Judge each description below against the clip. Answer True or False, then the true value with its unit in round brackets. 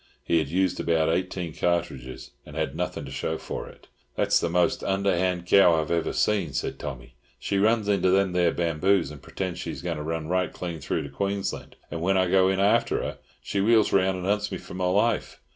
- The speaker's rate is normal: False (215 wpm)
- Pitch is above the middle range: False (90 Hz)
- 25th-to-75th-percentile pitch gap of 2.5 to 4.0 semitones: True (2.9 semitones)